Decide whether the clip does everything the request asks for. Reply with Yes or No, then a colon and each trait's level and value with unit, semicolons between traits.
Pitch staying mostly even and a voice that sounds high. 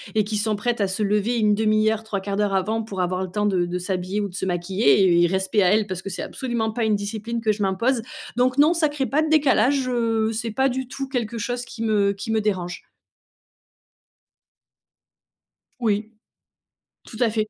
No: average, 3.1 semitones; high, 215 Hz